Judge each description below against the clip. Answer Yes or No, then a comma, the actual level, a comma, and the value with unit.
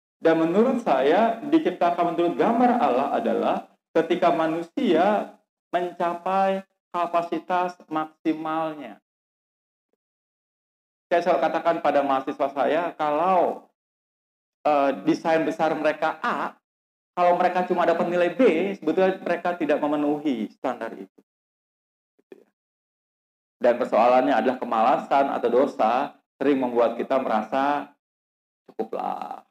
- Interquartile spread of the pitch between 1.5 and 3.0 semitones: Yes, narrow, 2.6 semitones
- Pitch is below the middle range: No, medium, 170 Hz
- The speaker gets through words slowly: No, average, 100 wpm